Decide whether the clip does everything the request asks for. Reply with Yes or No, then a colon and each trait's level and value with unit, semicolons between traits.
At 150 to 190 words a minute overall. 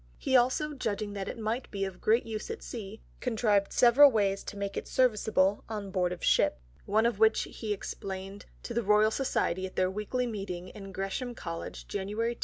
No: average, 200 wpm